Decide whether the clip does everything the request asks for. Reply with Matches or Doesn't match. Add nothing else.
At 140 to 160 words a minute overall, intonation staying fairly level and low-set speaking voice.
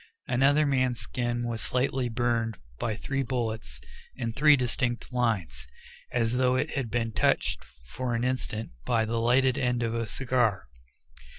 Matches